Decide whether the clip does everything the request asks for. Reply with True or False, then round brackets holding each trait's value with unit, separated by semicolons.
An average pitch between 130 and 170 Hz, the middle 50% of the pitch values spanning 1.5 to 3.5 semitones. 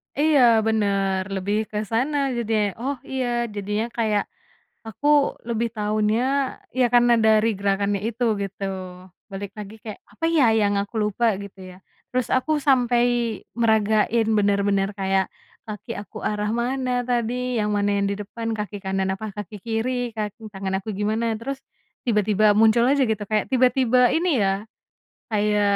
False (215 Hz; 2.8 semitones)